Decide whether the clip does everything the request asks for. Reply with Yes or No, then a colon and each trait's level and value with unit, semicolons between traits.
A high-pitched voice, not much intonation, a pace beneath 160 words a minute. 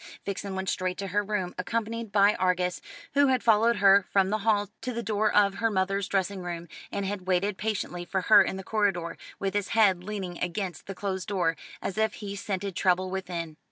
No: high, 195 Hz; narrow, 2.2 semitones; fast, 205 wpm